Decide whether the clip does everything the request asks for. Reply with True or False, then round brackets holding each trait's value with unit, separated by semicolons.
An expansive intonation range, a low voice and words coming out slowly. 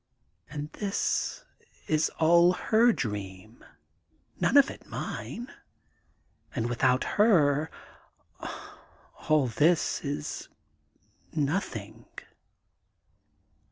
False (6.6 semitones; 150 Hz; 75 wpm)